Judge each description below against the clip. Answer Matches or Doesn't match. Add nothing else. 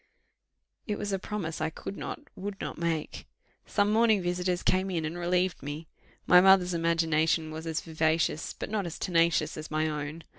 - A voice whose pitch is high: Doesn't match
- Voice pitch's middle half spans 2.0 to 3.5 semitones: Matches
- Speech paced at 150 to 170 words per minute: Doesn't match